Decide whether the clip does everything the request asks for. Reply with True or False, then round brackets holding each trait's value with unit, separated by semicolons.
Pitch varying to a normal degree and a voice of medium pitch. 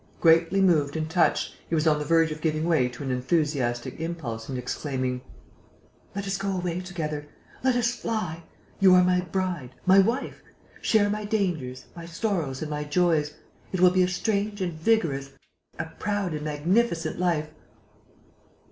True (4.2 semitones; 165 Hz)